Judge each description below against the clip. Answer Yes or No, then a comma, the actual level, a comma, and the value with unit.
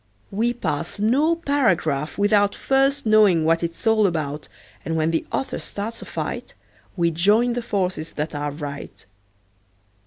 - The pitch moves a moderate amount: No, wide, 6.2 semitones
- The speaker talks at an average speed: Yes, average, 150 wpm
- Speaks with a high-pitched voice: Yes, high, 200 Hz